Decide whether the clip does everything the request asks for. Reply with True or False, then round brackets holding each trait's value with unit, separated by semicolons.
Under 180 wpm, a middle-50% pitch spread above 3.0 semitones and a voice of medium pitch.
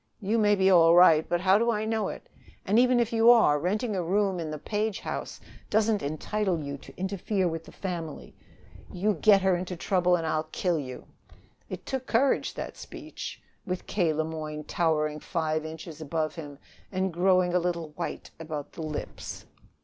False (190 wpm; 4.5 semitones; 180 Hz)